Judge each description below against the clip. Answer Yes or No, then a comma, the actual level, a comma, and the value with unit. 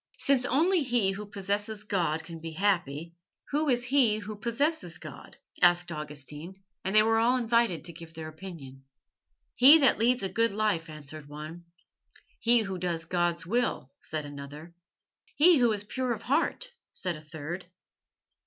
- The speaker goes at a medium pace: Yes, average, 160 wpm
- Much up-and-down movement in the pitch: Yes, wide, 6.4 semitones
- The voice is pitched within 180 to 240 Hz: Yes, high, 190 Hz